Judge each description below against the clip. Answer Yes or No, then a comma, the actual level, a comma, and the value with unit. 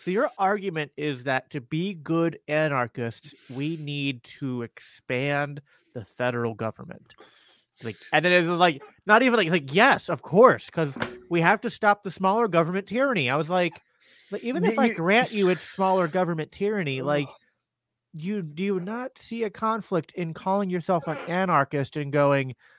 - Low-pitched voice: No, medium, 170 Hz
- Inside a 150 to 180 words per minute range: Yes, average, 175 wpm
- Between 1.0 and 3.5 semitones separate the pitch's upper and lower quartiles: No, wide, 5.4 semitones